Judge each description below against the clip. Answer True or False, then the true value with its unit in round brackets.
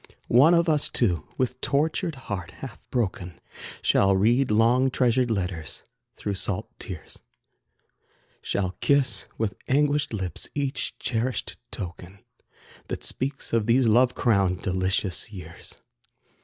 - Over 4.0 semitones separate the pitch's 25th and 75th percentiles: True (5.6 semitones)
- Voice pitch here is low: True (115 Hz)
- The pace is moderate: False (120 wpm)